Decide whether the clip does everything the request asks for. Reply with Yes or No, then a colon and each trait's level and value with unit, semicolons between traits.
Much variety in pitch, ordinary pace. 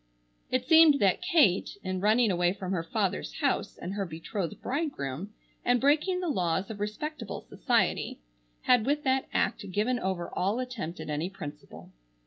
Yes: wide, 6.5 semitones; average, 160 wpm